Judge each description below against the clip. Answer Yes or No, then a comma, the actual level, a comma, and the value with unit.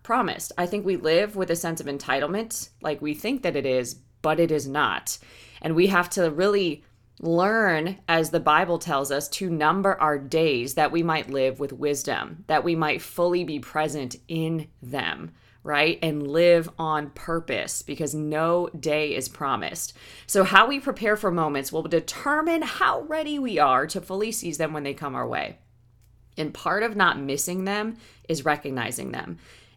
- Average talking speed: Yes, average, 180 wpm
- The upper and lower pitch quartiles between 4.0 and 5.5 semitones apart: Yes, average, 4.3 semitones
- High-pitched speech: No, medium, 160 Hz